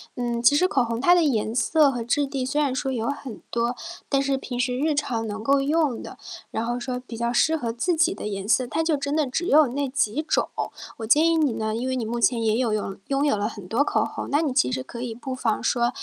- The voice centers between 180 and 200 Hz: No, very high, 255 Hz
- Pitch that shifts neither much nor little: Yes, average, 3.8 semitones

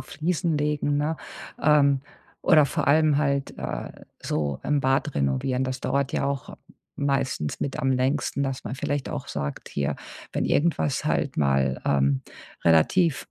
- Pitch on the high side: No, medium, 140 Hz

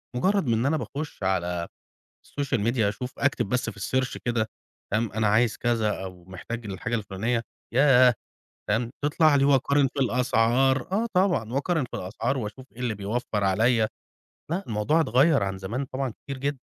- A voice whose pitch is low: Yes, low, 120 Hz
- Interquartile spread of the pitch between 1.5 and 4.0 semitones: No, average, 4.4 semitones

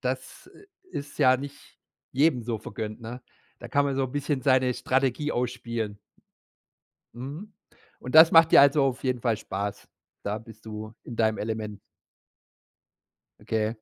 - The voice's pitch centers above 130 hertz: No, low, 125 Hz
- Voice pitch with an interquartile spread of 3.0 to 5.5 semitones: Yes, average, 3.9 semitones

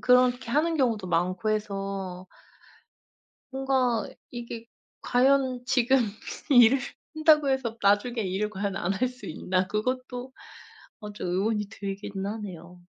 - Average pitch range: Yes, average, 4.4 semitones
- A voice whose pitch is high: Yes, high, 225 Hz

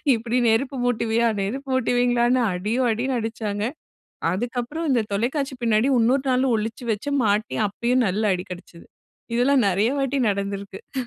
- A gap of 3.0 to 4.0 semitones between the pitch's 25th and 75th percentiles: Yes, average, 3.5 semitones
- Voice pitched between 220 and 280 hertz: Yes, high, 235 Hz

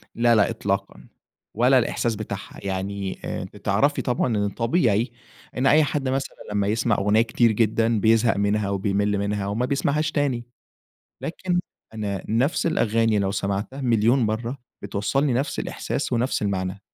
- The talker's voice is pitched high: No, low, 110 Hz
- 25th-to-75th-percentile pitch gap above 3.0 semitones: Yes, average, 3.8 semitones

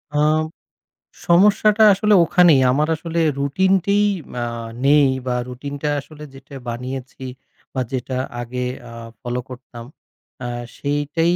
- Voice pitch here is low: No, medium, 145 Hz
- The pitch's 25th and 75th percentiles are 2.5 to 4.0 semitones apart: No, average, 5.0 semitones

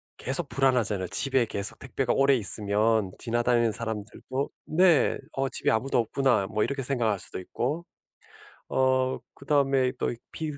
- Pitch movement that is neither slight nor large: Yes, average, 3.6 semitones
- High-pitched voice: No, low, 125 Hz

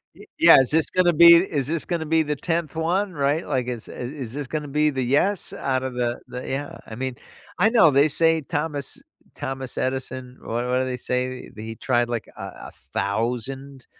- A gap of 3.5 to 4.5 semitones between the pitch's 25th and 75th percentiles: Yes, average, 4.1 semitones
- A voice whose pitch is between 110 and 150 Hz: Yes, low, 135 Hz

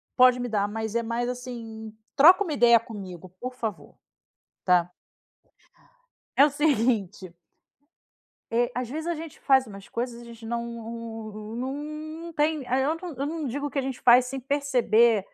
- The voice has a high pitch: Yes, high, 240 Hz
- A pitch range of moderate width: Yes, average, 3.5 semitones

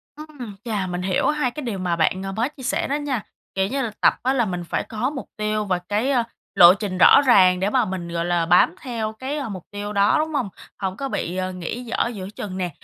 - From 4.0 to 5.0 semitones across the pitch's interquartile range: No, wide, 5.6 semitones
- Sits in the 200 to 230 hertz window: Yes, high, 210 Hz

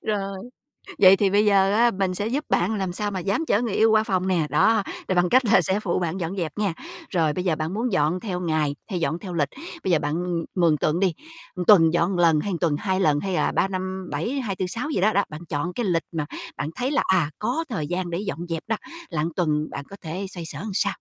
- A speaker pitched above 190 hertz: No, medium, 185 Hz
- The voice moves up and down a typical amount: Yes, average, 3.4 semitones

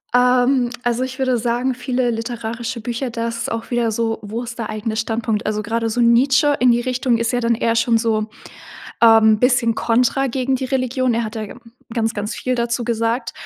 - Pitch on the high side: Yes, high, 235 Hz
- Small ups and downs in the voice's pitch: Yes, narrow, 1.7 semitones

